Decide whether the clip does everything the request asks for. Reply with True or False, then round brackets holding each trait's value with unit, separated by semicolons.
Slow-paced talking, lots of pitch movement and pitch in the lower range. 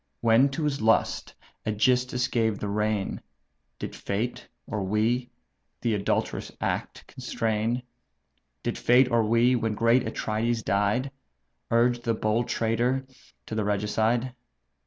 False (125 wpm; 2.4 semitones; 115 Hz)